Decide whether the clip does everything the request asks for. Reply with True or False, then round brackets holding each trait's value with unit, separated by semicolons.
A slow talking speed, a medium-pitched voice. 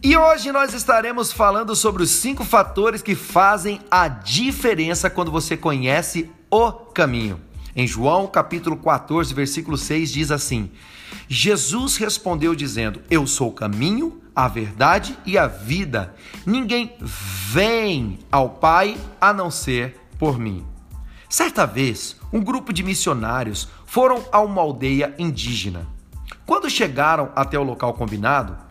False (135 wpm; 160 Hz)